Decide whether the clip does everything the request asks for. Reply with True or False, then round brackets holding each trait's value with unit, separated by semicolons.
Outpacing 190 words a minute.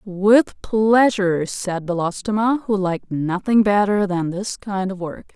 False (145 wpm)